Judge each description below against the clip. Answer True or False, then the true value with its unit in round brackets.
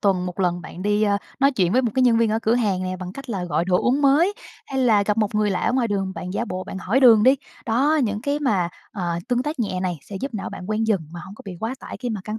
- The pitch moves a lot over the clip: False (5.0 semitones)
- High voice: True (210 Hz)